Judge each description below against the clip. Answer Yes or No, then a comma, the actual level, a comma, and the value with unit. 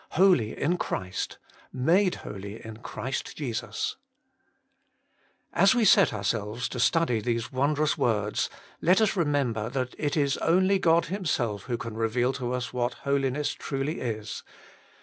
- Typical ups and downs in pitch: No, wide, 5.7 semitones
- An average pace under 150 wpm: Yes, average, 140 wpm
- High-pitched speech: No, low, 130 Hz